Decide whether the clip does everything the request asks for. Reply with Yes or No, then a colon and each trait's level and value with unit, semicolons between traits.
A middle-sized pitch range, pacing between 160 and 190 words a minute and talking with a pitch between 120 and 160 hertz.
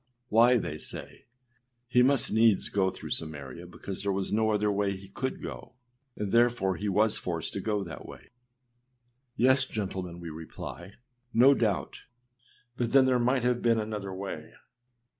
No: average, 4.1 semitones; average, 165 wpm; low, 105 Hz